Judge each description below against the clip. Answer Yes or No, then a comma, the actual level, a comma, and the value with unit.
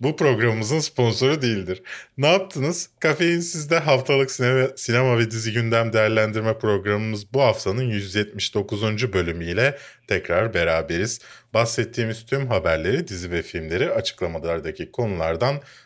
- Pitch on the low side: Yes, low, 115 Hz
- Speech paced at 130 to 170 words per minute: No, average, 115 wpm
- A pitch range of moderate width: Yes, average, 4.3 semitones